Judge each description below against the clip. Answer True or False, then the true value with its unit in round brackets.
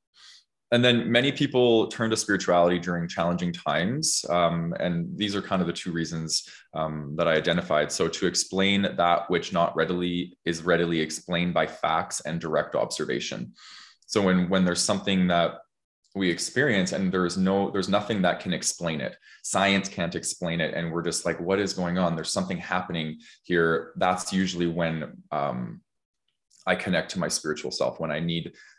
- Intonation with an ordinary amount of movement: False (2.3 semitones)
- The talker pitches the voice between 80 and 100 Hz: True (85 Hz)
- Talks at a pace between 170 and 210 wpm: True (175 wpm)